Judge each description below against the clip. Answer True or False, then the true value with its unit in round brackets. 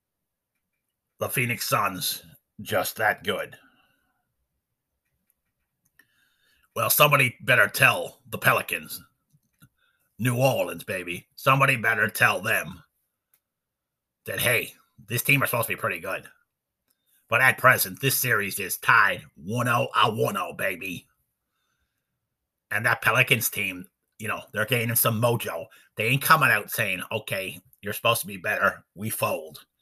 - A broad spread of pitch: False (3.4 semitones)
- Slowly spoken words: True (125 wpm)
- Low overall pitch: True (120 Hz)